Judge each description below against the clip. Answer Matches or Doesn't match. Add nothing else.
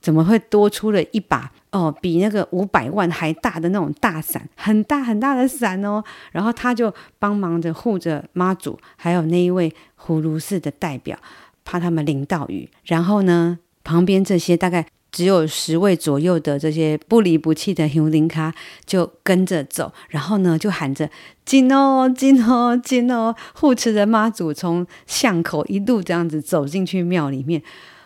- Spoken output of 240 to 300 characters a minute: Matches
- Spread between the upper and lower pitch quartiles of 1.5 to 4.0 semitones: Doesn't match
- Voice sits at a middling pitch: Matches